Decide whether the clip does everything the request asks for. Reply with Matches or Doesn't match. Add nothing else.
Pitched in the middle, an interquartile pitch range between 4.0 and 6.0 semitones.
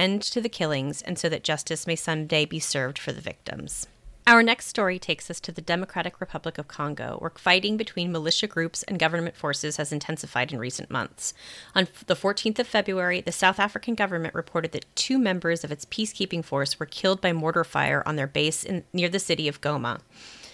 Doesn't match